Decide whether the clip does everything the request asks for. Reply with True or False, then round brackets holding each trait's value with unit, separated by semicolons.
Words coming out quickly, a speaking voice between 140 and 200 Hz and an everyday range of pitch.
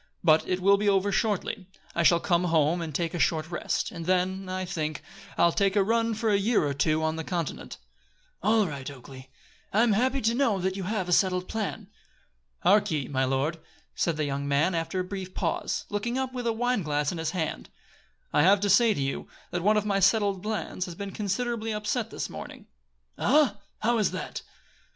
True (210 wpm; 190 Hz; 4.5 semitones)